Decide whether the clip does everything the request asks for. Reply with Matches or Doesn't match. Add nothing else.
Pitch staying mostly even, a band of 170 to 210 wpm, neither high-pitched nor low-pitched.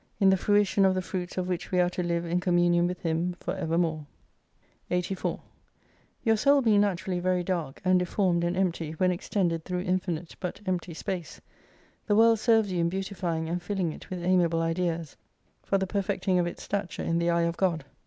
Matches